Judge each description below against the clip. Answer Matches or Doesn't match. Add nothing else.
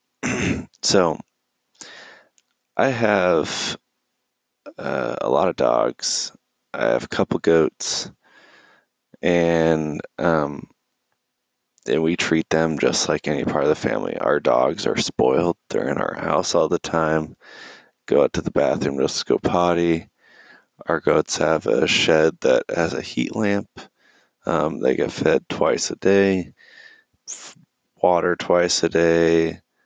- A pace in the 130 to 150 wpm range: Matches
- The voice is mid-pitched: Doesn't match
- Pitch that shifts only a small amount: Matches